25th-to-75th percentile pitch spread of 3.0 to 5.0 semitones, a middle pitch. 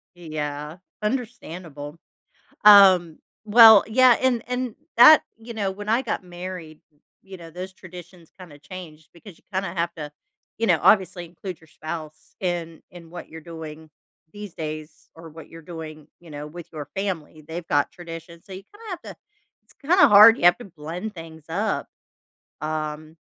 Yes: average, 4.0 semitones; medium, 175 Hz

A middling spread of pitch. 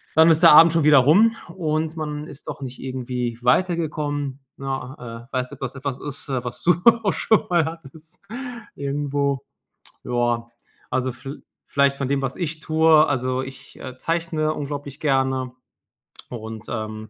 Yes: average, 3.5 semitones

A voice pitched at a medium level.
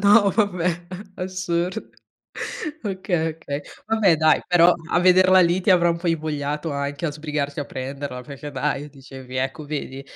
Yes: medium, 160 Hz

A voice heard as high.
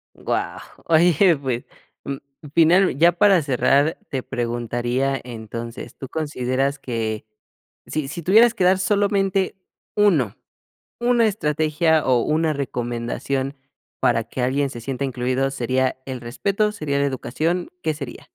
No: medium, 140 Hz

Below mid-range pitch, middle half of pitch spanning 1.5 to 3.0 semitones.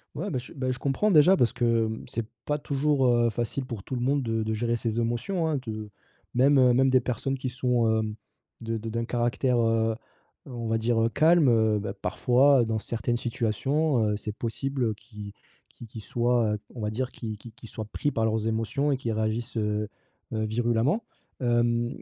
Yes: low, 120 Hz; average, 2.7 semitones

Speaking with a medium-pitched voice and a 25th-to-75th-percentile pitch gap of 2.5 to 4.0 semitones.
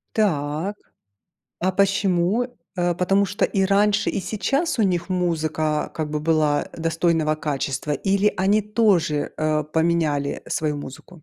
No: medium, 175 Hz; average, 4.4 semitones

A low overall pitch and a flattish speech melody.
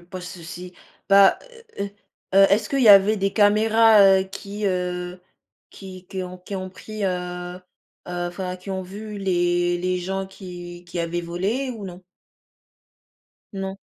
No: high, 190 Hz; narrow, 2.0 semitones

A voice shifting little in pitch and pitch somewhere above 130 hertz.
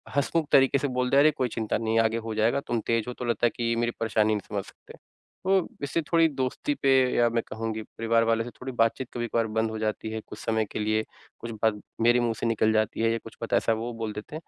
No: narrow, 2.3 semitones; low, 115 Hz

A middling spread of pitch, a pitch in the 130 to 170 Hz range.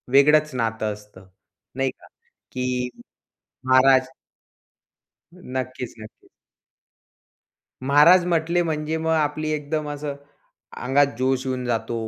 Yes: average, 3.3 semitones; low, 135 Hz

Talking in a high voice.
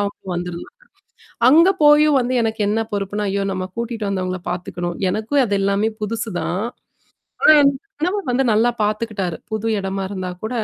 Yes: high, 210 Hz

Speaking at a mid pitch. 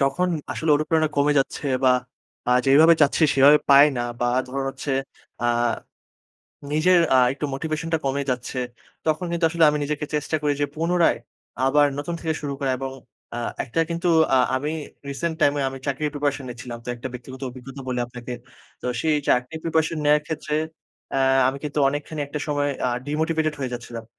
Yes: medium, 145 Hz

